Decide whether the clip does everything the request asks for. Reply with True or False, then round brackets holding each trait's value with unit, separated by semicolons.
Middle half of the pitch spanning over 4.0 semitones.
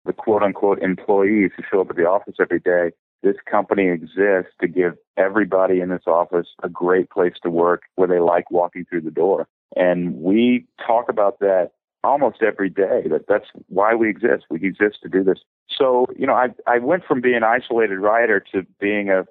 False (3.4 semitones)